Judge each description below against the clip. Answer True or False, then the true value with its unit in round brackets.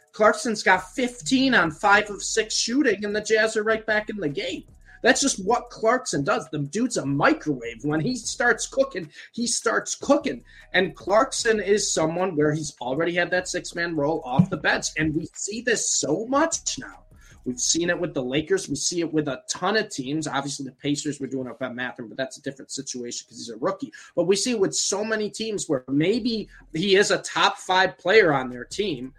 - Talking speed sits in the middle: False (220 wpm)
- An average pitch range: False (7.0 semitones)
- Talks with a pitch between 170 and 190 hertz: True (180 Hz)